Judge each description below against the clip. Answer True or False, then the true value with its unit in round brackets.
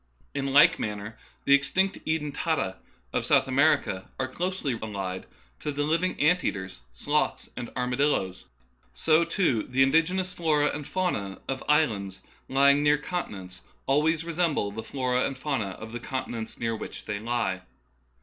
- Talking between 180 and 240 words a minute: False (150 wpm)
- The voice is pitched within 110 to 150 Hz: True (135 Hz)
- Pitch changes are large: True (6.3 semitones)